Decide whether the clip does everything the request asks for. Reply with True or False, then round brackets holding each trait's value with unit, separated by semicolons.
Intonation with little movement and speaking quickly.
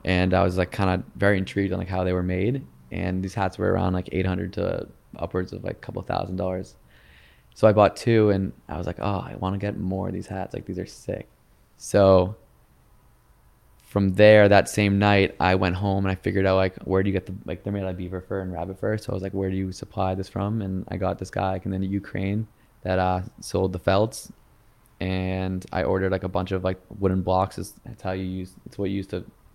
True (1.3 semitones; 250 wpm)